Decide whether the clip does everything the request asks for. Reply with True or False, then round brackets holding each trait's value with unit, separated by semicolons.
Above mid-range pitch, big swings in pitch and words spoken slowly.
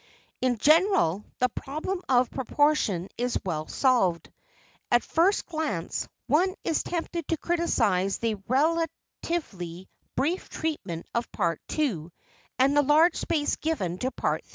True (265 Hz; 8.6 semitones; 130 wpm)